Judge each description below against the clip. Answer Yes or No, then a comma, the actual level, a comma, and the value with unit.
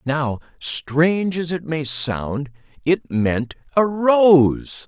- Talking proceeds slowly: Yes, slow, 100 wpm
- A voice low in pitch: No, medium, 150 Hz